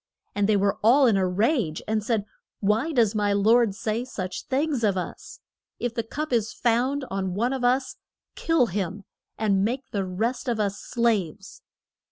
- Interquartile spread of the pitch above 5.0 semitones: No, average, 3.6 semitones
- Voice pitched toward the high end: Yes, high, 220 Hz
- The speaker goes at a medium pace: Yes, average, 180 wpm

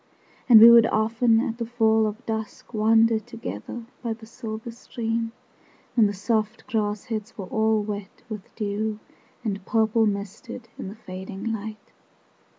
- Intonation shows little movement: Yes, narrow, 1.4 semitones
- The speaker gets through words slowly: No, average, 155 wpm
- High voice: Yes, high, 220 Hz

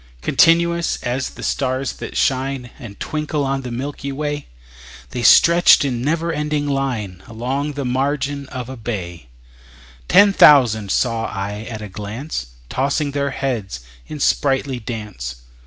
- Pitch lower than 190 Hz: Yes, low, 135 Hz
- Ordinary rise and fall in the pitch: Yes, average, 4.2 semitones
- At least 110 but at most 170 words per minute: Yes, average, 140 wpm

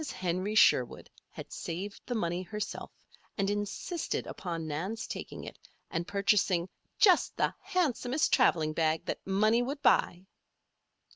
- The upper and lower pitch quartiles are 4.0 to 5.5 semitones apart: Yes, average, 4.7 semitones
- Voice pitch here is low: No, high, 195 Hz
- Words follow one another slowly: Yes, slow, 130 wpm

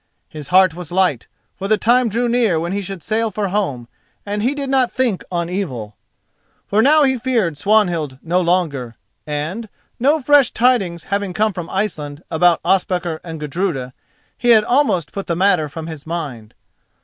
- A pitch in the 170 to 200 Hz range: Yes, medium, 185 Hz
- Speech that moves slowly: No, average, 175 wpm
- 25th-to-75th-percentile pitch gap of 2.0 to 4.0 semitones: No, average, 5.3 semitones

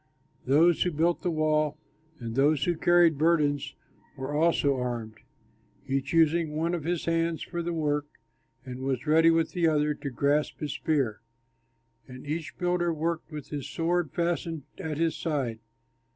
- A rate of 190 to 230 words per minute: No, average, 160 wpm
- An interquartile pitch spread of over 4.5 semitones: No, average, 2.8 semitones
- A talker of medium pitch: Yes, medium, 155 Hz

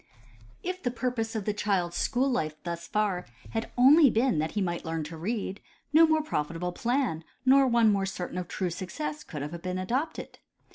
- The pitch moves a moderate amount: No, wide, 6.7 semitones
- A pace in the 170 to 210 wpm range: Yes, average, 190 wpm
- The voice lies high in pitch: Yes, high, 205 Hz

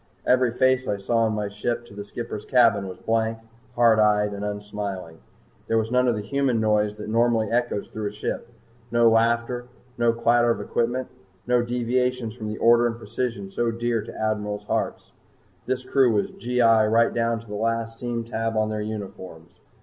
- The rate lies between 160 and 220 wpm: Yes, average, 190 wpm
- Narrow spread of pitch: Yes, narrow, 2.1 semitones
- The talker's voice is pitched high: No, low, 115 Hz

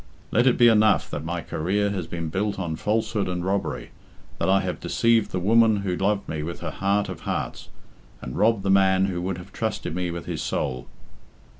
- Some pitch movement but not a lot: Yes, average, 3.0 semitones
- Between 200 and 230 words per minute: Yes, fast, 205 wpm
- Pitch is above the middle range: No, very low, 95 Hz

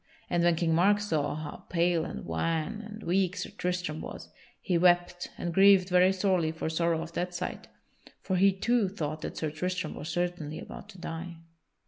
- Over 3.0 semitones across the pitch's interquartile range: No, narrow, 2.4 semitones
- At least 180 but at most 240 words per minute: Yes, average, 185 wpm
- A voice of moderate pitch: Yes, medium, 175 Hz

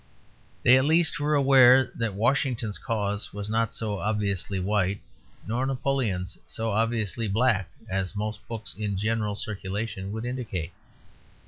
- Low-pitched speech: Yes, low, 110 Hz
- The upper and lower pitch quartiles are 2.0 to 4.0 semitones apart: Yes, average, 3.3 semitones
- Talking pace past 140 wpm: No, slow, 135 wpm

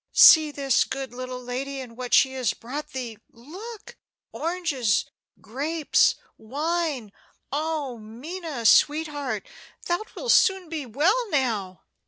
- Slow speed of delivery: Yes, slow, 120 wpm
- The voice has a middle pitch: No, very high, 280 Hz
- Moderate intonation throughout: Yes, average, 4.6 semitones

